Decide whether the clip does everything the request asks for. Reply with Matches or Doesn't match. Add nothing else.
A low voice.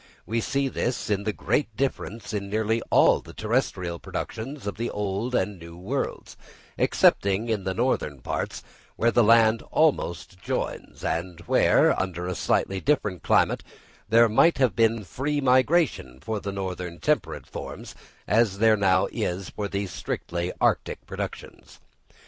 Matches